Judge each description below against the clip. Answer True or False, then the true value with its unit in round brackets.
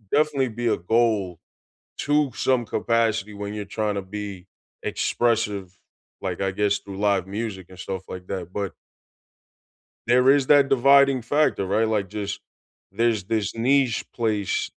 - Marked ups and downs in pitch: False (3.5 semitones)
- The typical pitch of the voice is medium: False (105 Hz)